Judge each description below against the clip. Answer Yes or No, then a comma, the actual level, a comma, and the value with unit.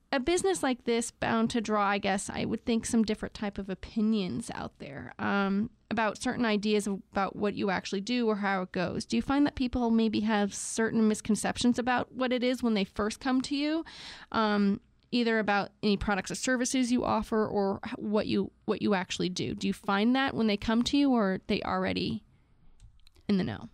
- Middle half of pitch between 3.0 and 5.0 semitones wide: Yes, average, 3.3 semitones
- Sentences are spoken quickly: Yes, fast, 210 wpm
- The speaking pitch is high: Yes, high, 220 Hz